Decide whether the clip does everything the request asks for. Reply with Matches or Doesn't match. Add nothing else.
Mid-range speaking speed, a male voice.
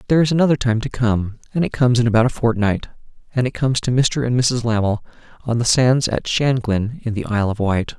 Doesn't match